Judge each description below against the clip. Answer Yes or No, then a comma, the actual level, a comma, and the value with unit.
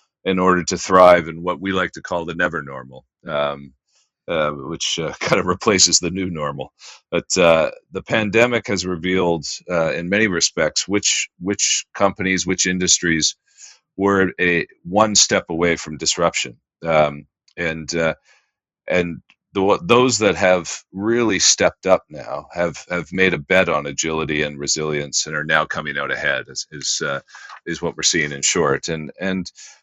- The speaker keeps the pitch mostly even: No, average, 3.1 semitones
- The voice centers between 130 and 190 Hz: No, very low, 85 Hz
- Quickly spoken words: No, average, 165 wpm